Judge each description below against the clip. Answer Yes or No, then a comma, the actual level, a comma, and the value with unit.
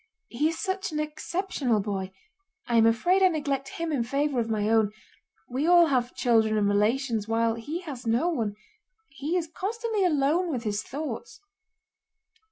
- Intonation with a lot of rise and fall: Yes, wide, 6.7 semitones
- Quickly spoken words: No, average, 170 wpm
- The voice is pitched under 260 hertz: No, very high, 275 Hz